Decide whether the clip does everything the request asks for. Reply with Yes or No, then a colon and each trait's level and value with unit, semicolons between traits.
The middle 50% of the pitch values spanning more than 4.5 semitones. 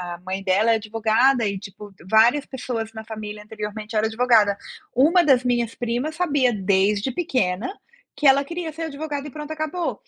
Yes: average, 5.1 semitones